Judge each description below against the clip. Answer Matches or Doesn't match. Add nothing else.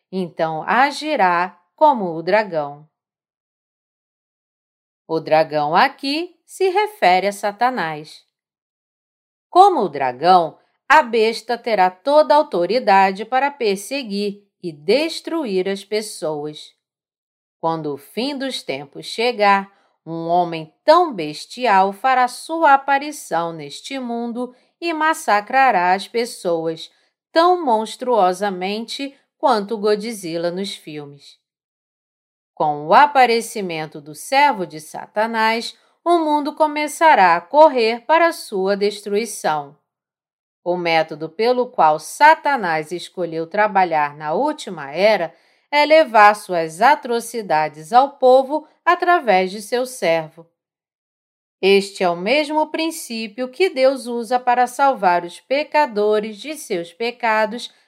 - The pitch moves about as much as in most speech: Doesn't match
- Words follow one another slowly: Matches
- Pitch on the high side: Matches